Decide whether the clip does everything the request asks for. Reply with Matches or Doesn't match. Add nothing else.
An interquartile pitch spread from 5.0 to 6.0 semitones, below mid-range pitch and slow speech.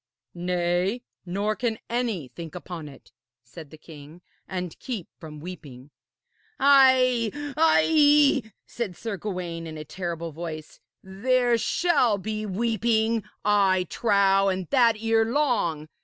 Doesn't match